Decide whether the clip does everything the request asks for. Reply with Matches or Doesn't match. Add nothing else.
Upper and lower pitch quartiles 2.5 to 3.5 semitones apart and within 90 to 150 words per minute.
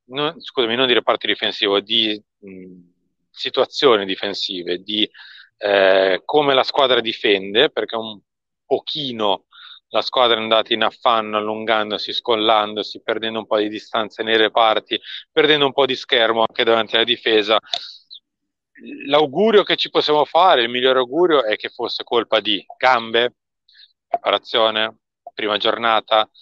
Matches